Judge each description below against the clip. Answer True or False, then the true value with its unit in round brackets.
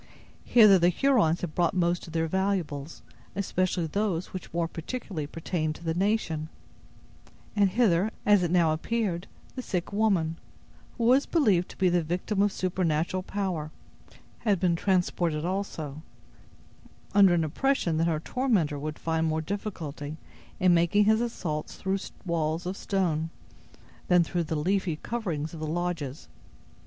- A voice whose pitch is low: False (175 Hz)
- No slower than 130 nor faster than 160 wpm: True (150 wpm)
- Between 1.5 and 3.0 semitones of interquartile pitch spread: False (3.7 semitones)